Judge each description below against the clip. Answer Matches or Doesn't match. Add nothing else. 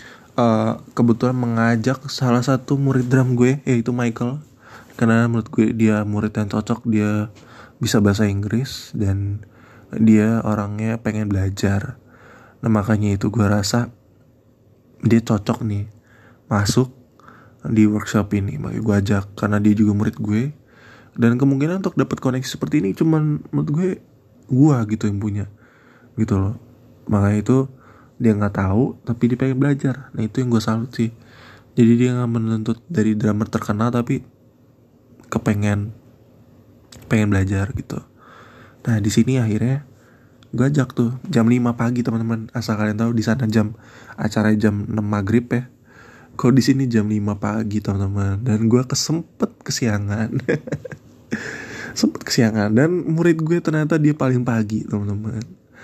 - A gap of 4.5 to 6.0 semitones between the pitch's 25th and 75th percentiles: Doesn't match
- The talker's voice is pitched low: Matches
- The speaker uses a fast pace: Matches